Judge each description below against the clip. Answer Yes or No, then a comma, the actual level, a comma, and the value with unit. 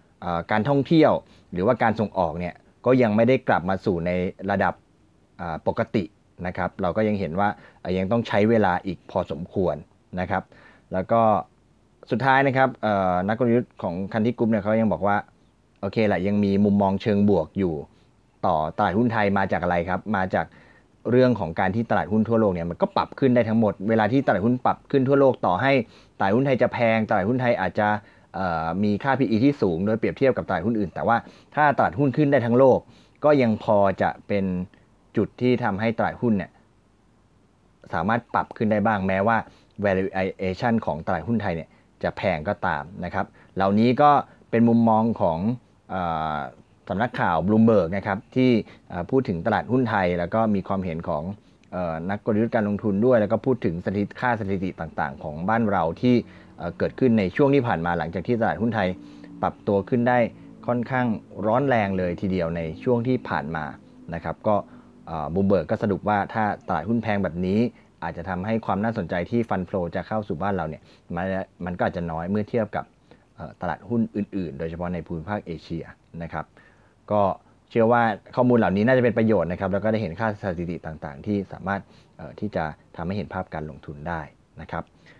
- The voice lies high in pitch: No, low, 105 Hz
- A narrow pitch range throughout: No, average, 3.9 semitones